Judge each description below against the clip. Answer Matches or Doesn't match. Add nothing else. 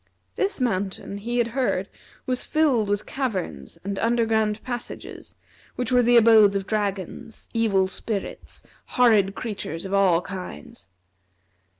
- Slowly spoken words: Matches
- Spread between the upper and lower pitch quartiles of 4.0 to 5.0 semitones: Doesn't match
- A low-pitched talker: Doesn't match